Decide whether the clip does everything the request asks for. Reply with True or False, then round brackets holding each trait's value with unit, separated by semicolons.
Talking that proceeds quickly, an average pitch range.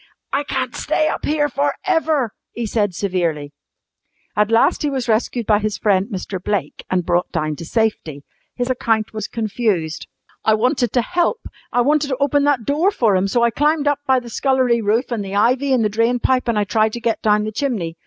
True (215 wpm; 4.4 semitones)